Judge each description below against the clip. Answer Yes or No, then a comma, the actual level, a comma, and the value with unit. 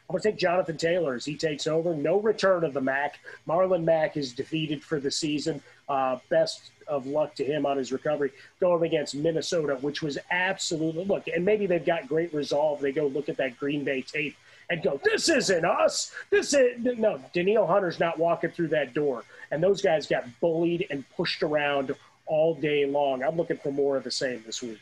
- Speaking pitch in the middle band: Yes, medium, 160 Hz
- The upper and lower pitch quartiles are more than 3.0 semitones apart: Yes, average, 3.8 semitones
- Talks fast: Yes, fast, 210 wpm